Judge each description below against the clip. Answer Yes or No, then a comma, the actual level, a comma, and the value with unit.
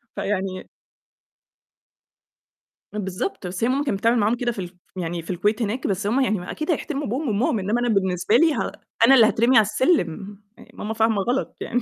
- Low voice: No, high, 220 Hz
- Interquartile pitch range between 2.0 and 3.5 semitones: No, average, 4.1 semitones